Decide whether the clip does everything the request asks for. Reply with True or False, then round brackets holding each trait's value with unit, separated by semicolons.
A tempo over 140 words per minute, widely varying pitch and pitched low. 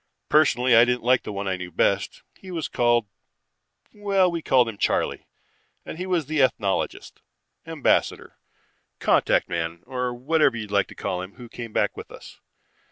True (170 wpm; 7.1 semitones; 120 Hz)